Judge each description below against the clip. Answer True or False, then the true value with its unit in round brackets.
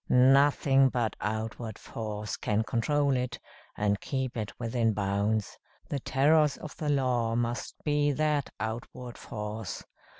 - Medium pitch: False (120 Hz)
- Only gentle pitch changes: False (4.0 semitones)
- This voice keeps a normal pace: False (130 wpm)